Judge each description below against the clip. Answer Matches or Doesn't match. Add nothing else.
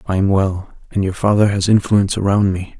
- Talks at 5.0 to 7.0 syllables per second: Matches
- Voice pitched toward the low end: Matches